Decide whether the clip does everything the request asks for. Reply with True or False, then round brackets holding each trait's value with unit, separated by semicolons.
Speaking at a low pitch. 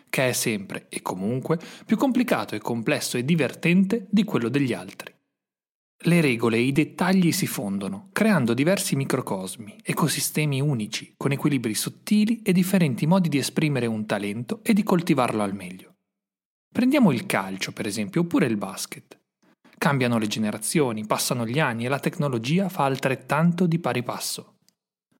False (145 Hz)